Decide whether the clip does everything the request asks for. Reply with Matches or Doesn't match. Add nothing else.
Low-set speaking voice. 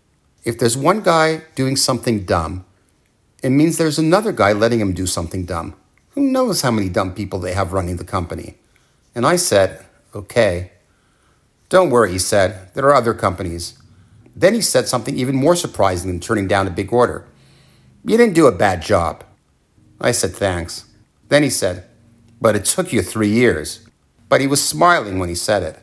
Matches